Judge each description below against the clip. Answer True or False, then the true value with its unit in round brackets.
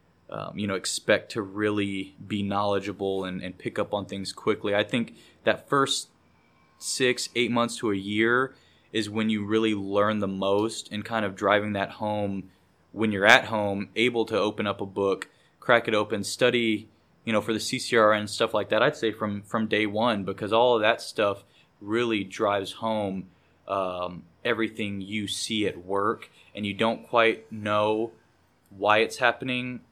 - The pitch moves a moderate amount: False (2.3 semitones)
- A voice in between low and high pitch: False (105 Hz)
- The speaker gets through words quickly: False (180 wpm)